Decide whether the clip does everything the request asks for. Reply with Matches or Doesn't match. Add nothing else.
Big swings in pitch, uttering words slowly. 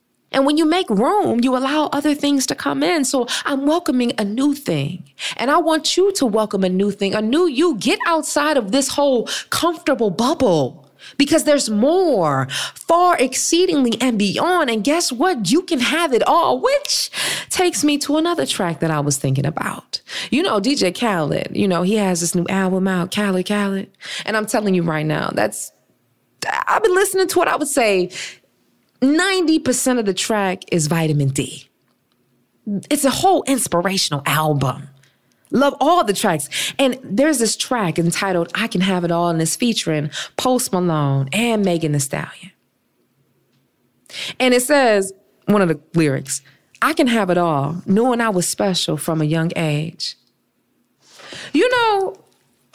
Doesn't match